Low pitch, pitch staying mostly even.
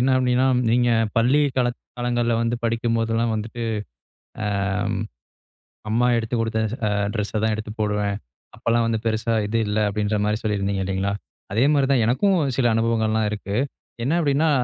Yes: low, 115 Hz; narrow, 2.2 semitones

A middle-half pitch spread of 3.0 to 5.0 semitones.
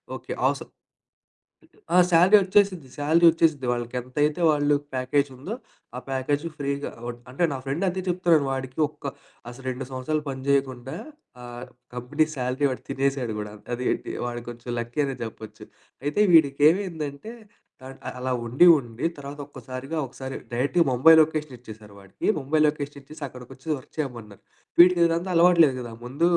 Yes: average, 3.7 semitones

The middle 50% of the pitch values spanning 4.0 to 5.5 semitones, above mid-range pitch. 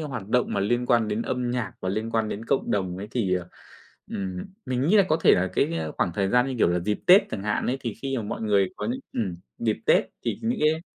No: average, 4.3 semitones; low, 110 Hz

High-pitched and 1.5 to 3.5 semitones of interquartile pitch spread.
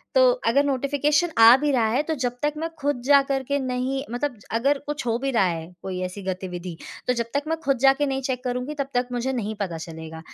No: very high, 255 Hz; average, 4.3 semitones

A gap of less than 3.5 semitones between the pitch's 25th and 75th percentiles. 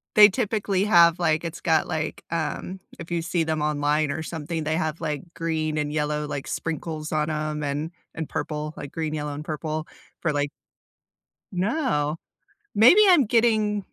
Yes: narrow, 2.5 semitones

